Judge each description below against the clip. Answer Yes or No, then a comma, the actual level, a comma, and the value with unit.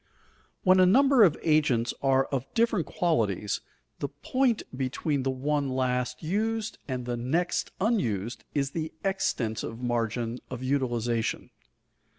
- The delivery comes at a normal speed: No, slow, 130 wpm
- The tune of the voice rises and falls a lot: Yes, wide, 6.6 semitones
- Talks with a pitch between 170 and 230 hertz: No, low, 135 Hz